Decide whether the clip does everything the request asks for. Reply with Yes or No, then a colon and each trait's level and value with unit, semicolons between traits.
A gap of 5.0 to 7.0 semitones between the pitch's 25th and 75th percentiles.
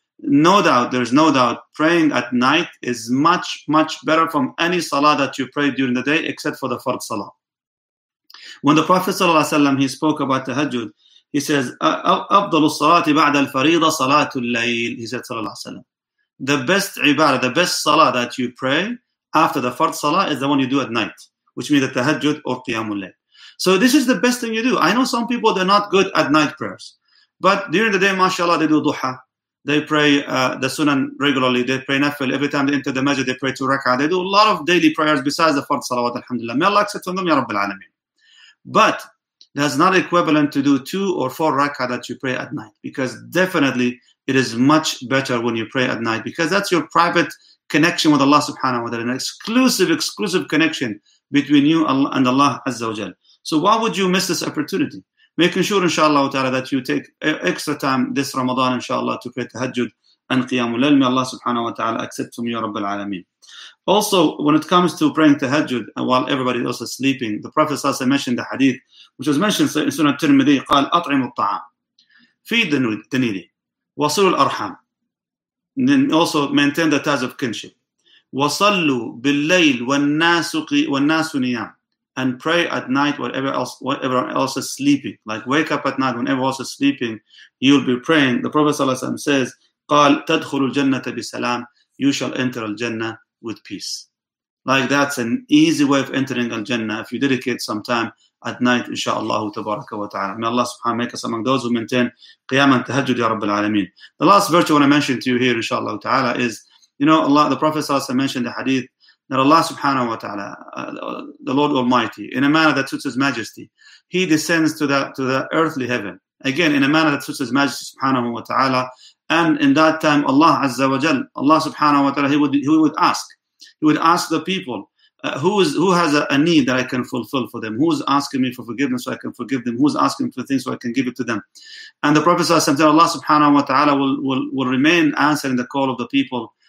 No: average, 4.3 semitones